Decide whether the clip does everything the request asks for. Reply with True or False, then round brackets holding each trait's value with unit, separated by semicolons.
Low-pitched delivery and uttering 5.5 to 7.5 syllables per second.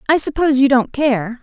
False (265 Hz; 5.7 syllables/s)